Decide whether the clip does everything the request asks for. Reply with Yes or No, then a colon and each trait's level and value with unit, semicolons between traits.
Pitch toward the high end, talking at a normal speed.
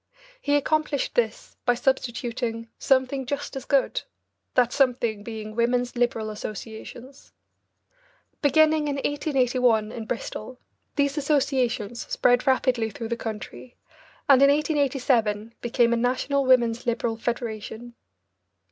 No: high, 245 Hz; slow, 115 wpm